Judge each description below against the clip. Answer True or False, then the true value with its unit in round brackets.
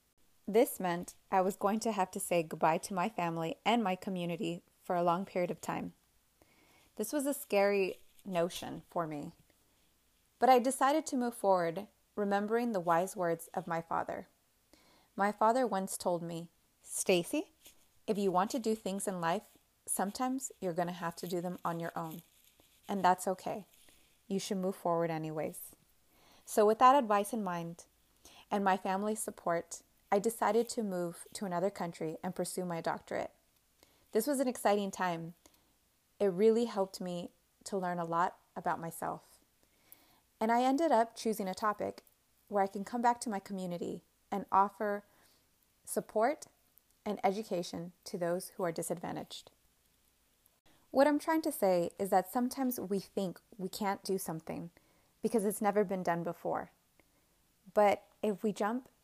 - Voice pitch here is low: False (195 Hz)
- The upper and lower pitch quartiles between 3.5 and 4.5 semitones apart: True (3.9 semitones)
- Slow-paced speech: False (165 wpm)